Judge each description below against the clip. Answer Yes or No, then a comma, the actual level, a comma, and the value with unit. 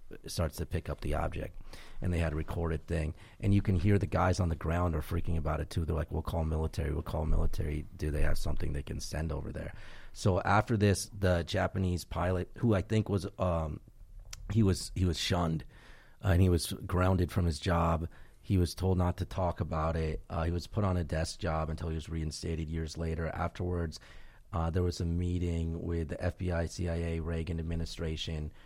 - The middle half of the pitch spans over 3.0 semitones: No, narrow, 2.6 semitones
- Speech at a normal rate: No, fast, 210 wpm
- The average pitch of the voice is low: Yes, very low, 85 Hz